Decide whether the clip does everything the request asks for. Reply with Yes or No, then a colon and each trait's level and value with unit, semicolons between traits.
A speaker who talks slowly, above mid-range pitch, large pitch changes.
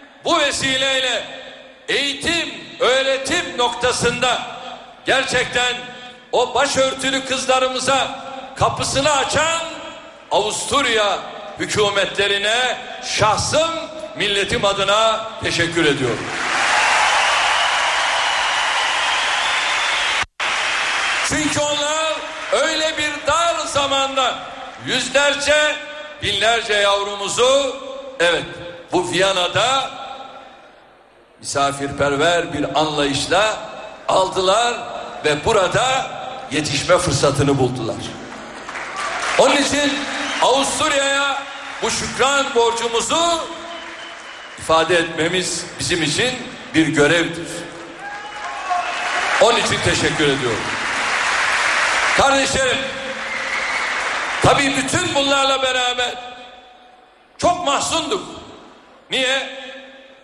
Yes: slow, 65 wpm; very high, 265 Hz; wide, 6.5 semitones